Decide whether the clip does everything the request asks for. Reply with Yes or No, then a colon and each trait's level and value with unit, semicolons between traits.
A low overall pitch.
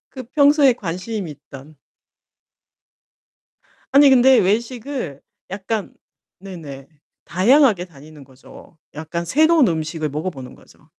No: medium, 185 Hz